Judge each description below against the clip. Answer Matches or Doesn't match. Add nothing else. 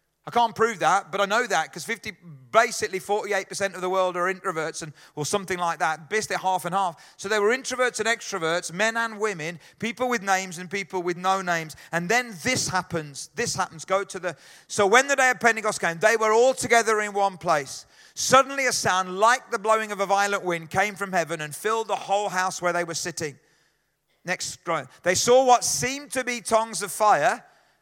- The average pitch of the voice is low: Doesn't match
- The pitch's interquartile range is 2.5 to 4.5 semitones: Matches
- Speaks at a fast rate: Matches